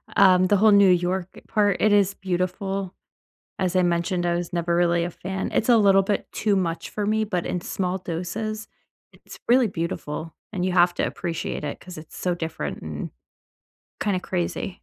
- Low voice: No, medium, 185 Hz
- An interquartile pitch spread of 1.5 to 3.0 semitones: Yes, narrow, 2.4 semitones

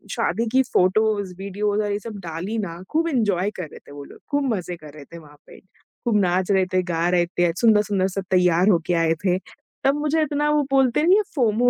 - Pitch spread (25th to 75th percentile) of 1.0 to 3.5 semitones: No, average, 5.1 semitones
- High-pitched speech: Yes, high, 200 Hz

